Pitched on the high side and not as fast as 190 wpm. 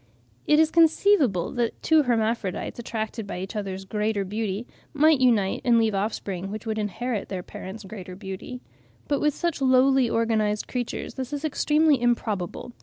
Yes: high, 225 Hz; average, 160 wpm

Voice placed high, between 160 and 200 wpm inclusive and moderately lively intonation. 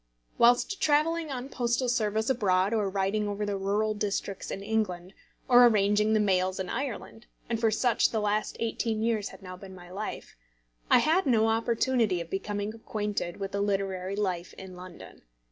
Yes: high, 210 Hz; average, 170 wpm; average, 3.0 semitones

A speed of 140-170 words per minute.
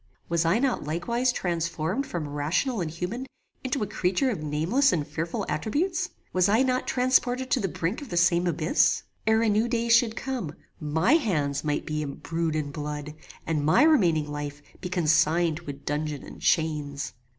No: average, 180 wpm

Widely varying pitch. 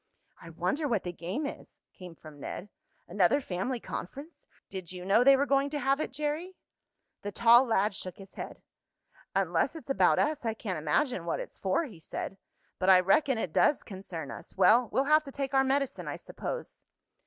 Yes: wide, 7.1 semitones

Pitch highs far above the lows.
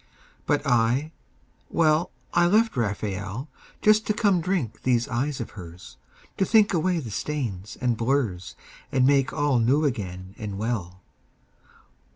Yes: wide, 6.7 semitones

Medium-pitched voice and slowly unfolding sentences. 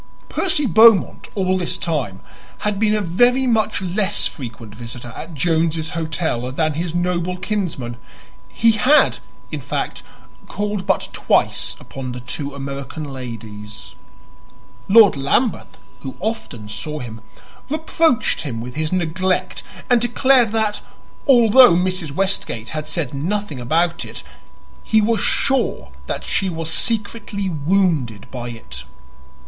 Yes: medium, 170 Hz; slow, 130 wpm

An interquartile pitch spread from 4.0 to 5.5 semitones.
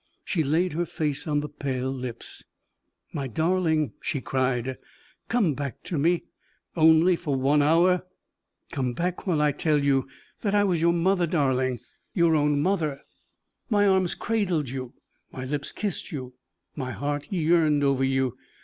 Yes: average, 4.4 semitones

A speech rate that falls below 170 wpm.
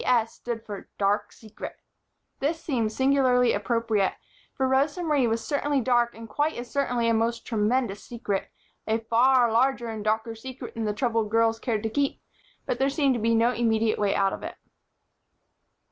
No: average, 175 wpm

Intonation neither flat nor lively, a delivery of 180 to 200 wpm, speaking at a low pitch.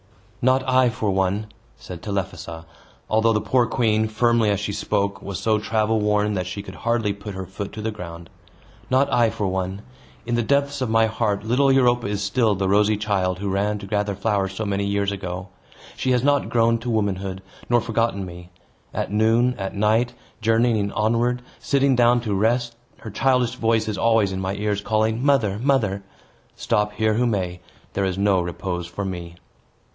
Yes: average, 3.1 semitones; average, 190 wpm; low, 105 Hz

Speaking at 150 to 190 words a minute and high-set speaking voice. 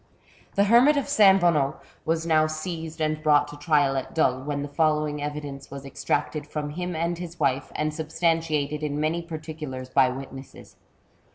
No: average, 170 wpm; medium, 155 Hz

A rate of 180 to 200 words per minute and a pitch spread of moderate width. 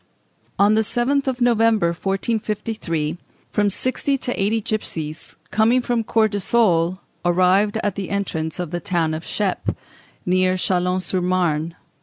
No: slow, 135 wpm; average, 4.0 semitones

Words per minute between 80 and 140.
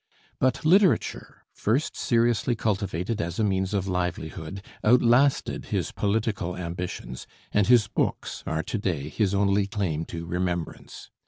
Yes: slow, 135 wpm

